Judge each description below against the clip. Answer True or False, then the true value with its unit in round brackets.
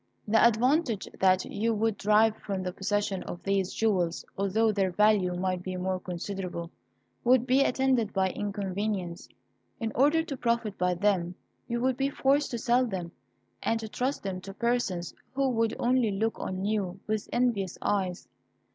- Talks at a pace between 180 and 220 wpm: False (165 wpm)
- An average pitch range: True (4.0 semitones)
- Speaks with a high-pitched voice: True (210 Hz)